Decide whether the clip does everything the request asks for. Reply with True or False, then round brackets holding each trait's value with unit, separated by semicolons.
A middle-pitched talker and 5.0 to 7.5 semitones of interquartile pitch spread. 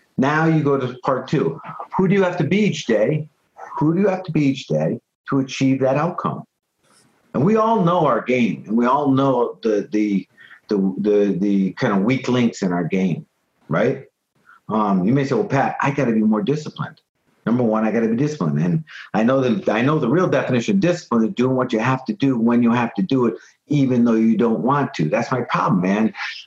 False (130 Hz; 5.6 semitones)